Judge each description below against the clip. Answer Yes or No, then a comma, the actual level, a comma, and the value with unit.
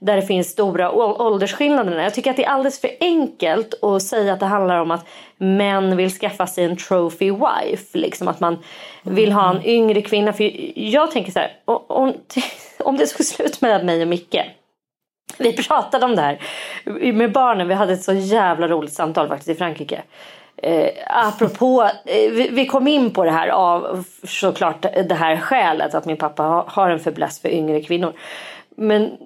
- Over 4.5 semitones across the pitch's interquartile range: Yes, wide, 5.6 semitones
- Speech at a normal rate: Yes, average, 180 wpm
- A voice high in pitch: Yes, high, 195 Hz